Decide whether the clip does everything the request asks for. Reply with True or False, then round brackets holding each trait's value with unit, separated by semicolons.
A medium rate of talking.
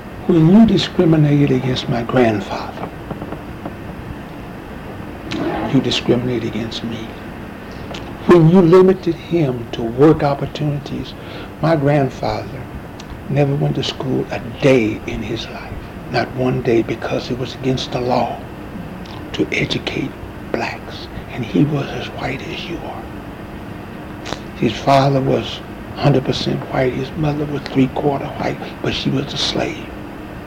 False (125 wpm)